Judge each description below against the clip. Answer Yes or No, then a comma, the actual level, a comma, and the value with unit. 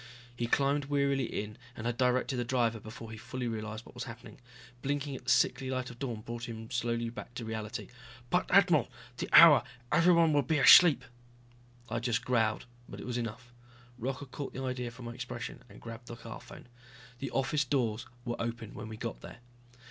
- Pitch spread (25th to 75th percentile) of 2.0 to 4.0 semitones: Yes, average, 2.7 semitones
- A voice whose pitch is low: Yes, low, 125 Hz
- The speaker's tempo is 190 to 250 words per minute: Yes, average, 195 wpm